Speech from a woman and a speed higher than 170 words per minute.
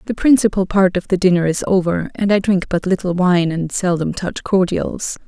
Yes: female; fast, 205 wpm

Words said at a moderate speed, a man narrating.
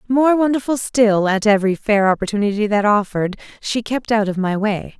No: average, 180 wpm; female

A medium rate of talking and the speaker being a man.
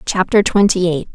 No: average, 160 wpm; female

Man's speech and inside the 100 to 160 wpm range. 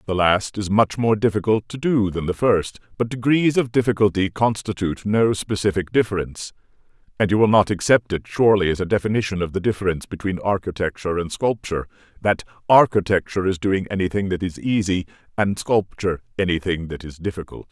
No: male; average, 170 wpm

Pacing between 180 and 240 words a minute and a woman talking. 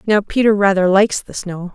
Yes: fast, 205 wpm; female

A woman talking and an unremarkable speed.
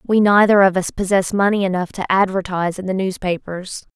Yes: female; average, 180 wpm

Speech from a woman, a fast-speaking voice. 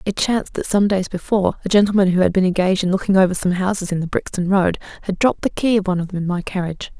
Yes: female; fast, 275 wpm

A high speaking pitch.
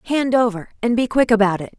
Yes: high, 225 Hz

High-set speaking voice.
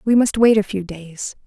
Yes: high, 205 Hz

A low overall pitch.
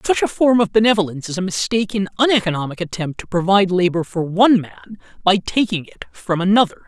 No: high, 190 Hz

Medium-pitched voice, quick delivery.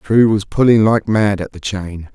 No: low, 105 Hz; fast, 225 wpm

